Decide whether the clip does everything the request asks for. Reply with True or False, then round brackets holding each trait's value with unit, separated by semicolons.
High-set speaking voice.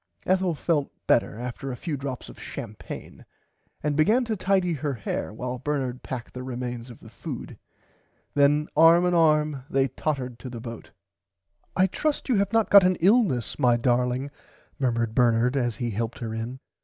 False (135 Hz)